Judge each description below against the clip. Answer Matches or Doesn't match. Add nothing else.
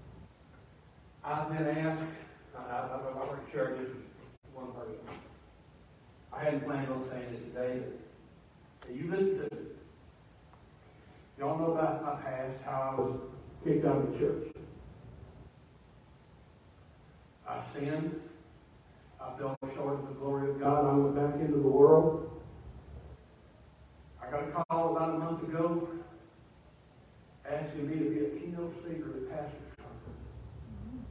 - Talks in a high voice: Doesn't match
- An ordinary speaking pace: Doesn't match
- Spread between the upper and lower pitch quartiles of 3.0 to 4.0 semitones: Matches